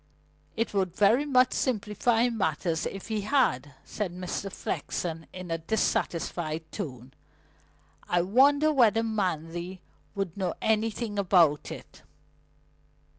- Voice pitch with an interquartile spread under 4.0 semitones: No, average, 5.0 semitones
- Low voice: No, high, 195 Hz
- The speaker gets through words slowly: Yes, slow, 115 wpm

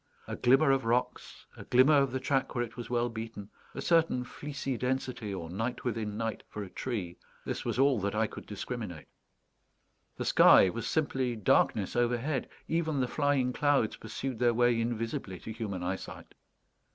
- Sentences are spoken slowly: No, average, 175 wpm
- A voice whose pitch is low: Yes, low, 120 Hz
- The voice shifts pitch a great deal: No, average, 3.2 semitones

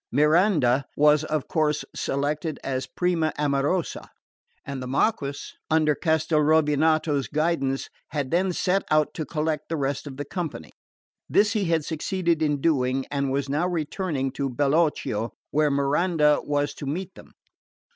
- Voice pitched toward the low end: No, medium, 150 Hz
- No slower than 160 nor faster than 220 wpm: No, average, 145 wpm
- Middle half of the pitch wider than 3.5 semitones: No, average, 2.7 semitones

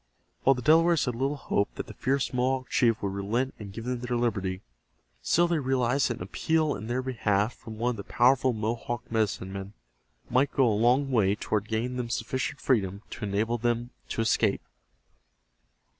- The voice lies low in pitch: Yes, low, 120 Hz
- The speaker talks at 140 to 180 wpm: No, average, 190 wpm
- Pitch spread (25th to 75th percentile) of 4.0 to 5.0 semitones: No, average, 3.3 semitones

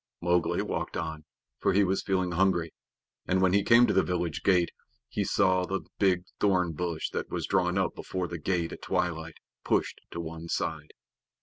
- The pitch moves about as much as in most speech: No, narrow, 2.3 semitones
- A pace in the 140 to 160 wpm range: No, average, 185 wpm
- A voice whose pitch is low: Yes, very low, 90 Hz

